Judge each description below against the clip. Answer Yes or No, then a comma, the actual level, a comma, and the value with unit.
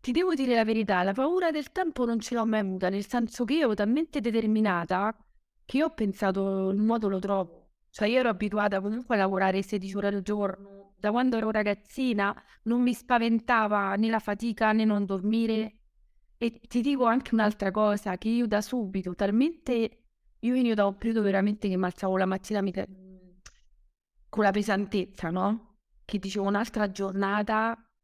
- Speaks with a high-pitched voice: Yes, high, 210 Hz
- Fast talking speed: Yes, fast, 175 wpm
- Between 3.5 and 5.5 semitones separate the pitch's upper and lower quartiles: No, average, 2.8 semitones